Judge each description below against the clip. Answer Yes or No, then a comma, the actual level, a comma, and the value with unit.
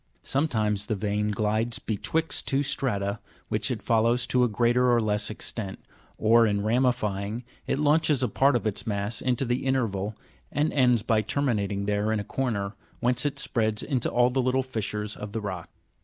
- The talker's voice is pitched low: Yes, low, 115 Hz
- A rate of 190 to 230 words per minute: No, average, 180 wpm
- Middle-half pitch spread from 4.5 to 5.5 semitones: No, average, 3.4 semitones